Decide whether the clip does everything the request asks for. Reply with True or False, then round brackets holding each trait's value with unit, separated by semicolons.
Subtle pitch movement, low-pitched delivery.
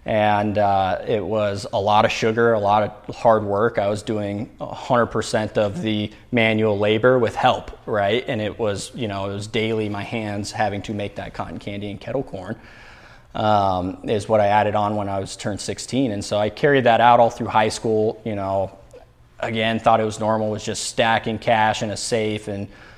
True (1.8 semitones; 105 Hz)